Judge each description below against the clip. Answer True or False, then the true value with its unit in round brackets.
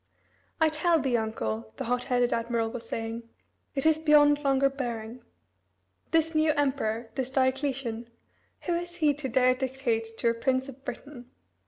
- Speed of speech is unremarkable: True (165 wpm)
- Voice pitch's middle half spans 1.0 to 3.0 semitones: False (3.9 semitones)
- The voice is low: False (260 Hz)